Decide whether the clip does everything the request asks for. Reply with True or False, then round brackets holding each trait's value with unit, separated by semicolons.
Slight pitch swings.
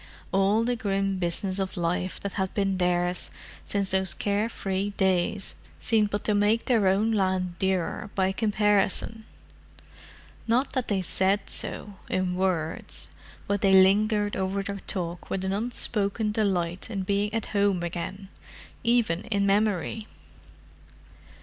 True (1.9 semitones)